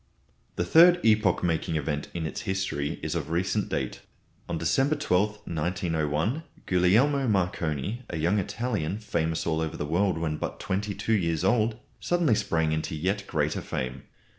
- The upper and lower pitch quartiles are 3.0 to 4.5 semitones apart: No, average, 5.1 semitones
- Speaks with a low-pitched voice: Yes, very low, 90 Hz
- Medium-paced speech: Yes, average, 160 wpm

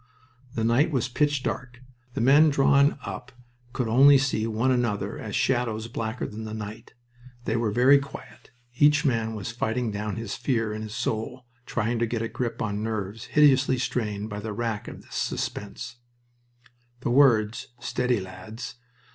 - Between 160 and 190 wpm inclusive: Yes, average, 165 wpm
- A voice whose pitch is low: Yes, low, 115 Hz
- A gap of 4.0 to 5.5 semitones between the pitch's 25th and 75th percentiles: No, average, 3.0 semitones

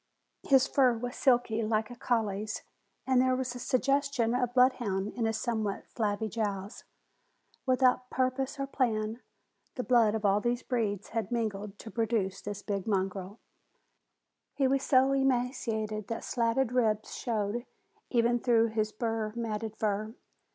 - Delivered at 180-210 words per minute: No, average, 145 wpm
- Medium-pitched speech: No, high, 230 Hz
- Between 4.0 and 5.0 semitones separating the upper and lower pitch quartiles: No, average, 2.9 semitones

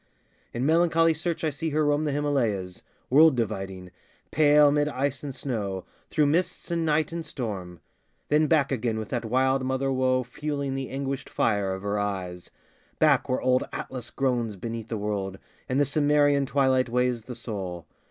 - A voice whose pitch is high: No, low, 130 Hz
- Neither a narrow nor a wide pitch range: Yes, average, 5.0 semitones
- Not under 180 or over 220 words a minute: No, average, 170 wpm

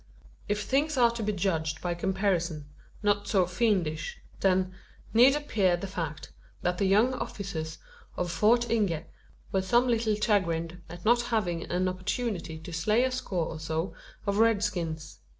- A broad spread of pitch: No, average, 4.6 semitones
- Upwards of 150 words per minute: Yes, average, 160 wpm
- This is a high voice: Yes, high, 195 Hz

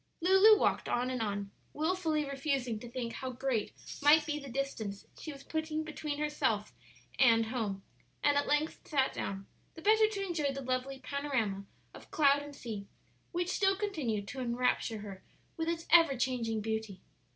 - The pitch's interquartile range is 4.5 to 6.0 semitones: Yes, average, 5.3 semitones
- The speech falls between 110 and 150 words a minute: No, average, 170 wpm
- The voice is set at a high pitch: Yes, very high, 275 Hz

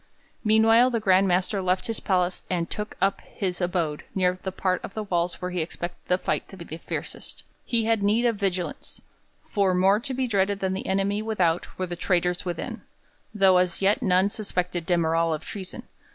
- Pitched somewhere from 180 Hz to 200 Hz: Yes, high, 190 Hz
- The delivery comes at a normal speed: Yes, average, 195 wpm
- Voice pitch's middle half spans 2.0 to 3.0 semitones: Yes, narrow, 2.5 semitones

